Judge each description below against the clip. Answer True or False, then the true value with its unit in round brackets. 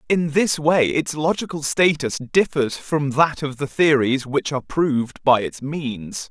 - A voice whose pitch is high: False (145 Hz)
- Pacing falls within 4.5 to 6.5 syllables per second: False (4.1 syllables/s)